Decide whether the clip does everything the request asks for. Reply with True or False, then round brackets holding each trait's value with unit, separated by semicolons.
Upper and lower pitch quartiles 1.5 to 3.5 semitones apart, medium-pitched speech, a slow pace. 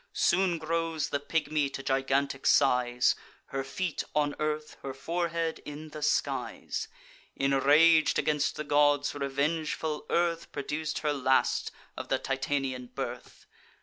True (2.6 semitones; 145 Hz; 125 wpm)